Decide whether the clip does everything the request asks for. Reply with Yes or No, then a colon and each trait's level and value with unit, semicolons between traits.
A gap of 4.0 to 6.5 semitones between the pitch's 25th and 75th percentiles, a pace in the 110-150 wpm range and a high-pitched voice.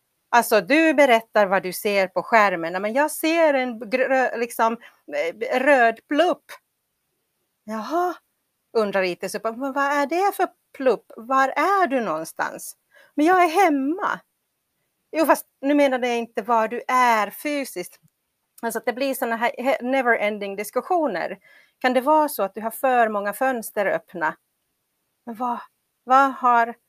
Yes: average, 4.8 semitones; average, 145 wpm; very high, 250 Hz